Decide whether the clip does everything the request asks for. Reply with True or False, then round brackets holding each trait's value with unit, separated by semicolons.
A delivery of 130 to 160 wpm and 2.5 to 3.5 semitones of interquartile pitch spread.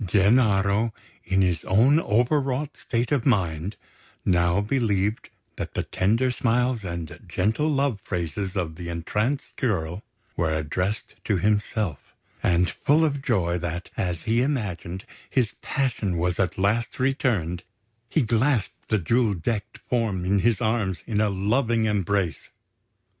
False (140 wpm; 4.9 semitones)